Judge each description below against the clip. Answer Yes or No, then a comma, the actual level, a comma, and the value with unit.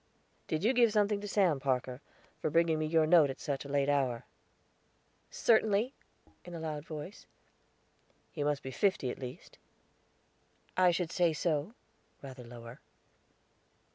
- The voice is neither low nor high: Yes, medium, 155 Hz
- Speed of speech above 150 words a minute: No, average, 145 wpm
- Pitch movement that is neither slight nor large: Yes, average, 5.0 semitones